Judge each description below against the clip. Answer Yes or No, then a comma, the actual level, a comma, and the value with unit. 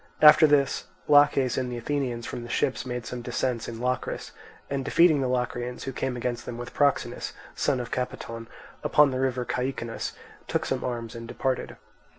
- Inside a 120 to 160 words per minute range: No, average, 175 wpm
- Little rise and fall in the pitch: Yes, narrow, 2.0 semitones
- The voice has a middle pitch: No, low, 125 Hz